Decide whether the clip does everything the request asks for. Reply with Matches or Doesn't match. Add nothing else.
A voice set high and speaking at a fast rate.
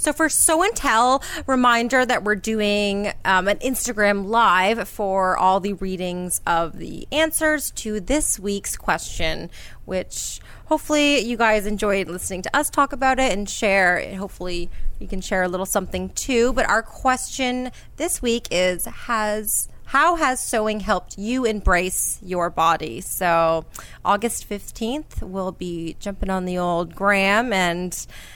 Doesn't match